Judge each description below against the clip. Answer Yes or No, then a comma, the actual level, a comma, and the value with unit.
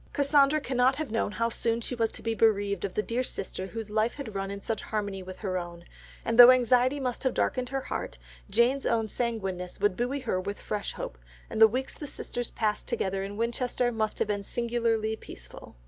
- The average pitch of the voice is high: Yes, high, 225 Hz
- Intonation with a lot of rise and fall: No, average, 3.5 semitones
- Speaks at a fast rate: Yes, fast, 210 wpm